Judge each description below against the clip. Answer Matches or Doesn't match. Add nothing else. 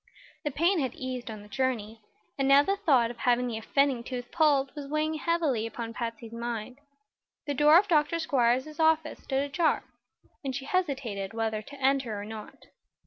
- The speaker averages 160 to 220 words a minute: Matches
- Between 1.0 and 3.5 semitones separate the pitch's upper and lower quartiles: Doesn't match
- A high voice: Matches